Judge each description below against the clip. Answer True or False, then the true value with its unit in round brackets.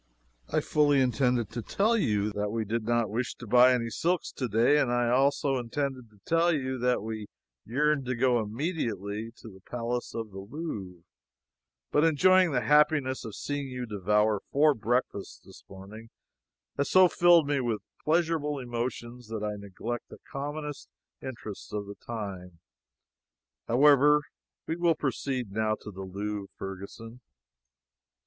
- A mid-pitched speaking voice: False (120 Hz)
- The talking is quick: False (155 wpm)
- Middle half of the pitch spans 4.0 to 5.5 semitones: True (5.1 semitones)